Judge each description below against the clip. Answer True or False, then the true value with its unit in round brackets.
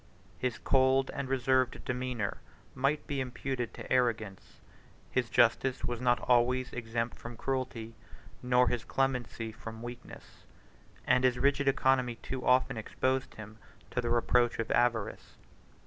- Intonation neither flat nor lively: False (1.8 semitones)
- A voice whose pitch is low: True (125 Hz)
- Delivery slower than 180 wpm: True (135 wpm)